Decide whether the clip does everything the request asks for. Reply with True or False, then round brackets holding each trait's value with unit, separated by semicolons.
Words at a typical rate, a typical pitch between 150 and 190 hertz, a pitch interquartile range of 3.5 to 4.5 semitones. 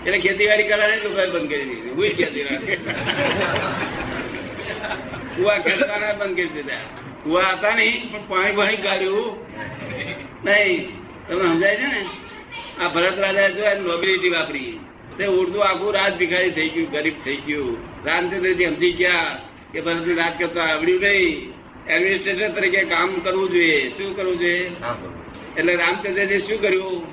False (145 wpm; 185 Hz; 2.8 semitones)